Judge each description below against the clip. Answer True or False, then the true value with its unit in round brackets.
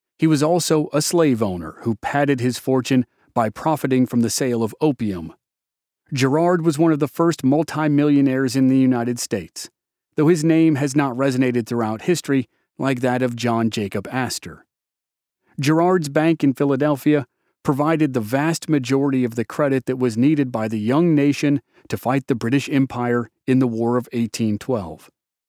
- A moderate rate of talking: True (165 wpm)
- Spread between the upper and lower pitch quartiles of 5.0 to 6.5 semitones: False (4.0 semitones)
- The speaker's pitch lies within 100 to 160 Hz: True (135 Hz)